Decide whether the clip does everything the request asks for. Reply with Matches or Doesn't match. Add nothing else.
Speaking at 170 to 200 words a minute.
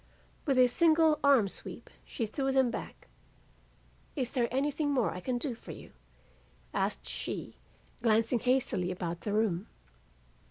Doesn't match